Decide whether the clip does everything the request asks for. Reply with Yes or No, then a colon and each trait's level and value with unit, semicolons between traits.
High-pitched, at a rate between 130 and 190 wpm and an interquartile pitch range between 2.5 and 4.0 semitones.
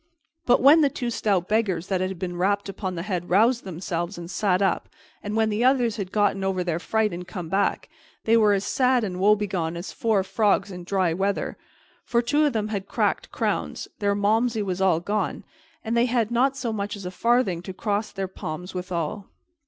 No: high, 200 Hz; fast, 205 wpm; average, 3.4 semitones